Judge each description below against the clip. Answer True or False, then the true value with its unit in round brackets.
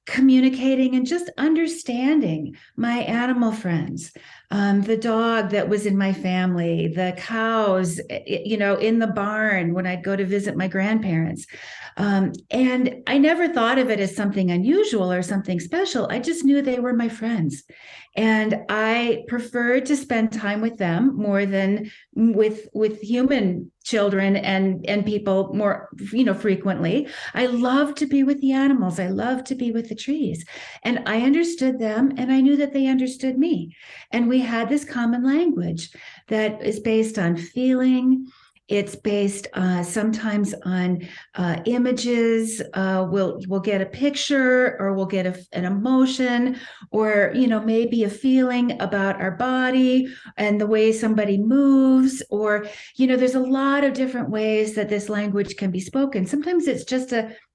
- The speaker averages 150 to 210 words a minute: True (165 wpm)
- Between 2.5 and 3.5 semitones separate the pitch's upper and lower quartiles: False (4.5 semitones)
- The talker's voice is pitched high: True (225 Hz)